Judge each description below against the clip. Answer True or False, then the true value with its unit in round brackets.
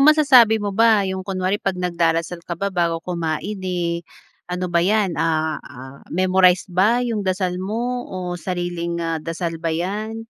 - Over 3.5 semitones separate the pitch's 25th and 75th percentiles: False (3.2 semitones)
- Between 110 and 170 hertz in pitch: False (185 Hz)